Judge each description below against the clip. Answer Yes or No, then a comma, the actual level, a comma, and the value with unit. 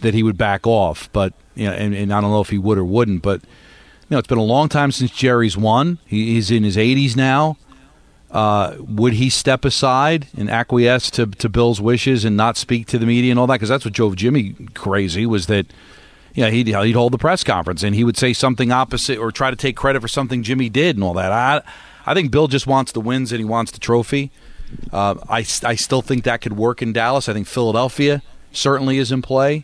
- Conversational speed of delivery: No, fast, 245 wpm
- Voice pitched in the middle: No, low, 120 Hz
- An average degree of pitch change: Yes, average, 3.2 semitones